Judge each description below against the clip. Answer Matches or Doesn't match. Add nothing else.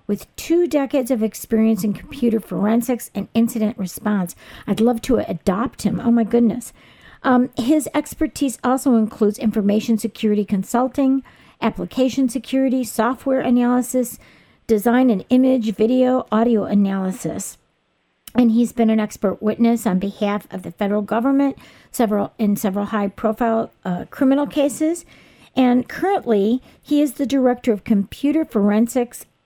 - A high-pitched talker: Matches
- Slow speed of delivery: Matches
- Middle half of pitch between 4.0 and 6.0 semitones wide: Doesn't match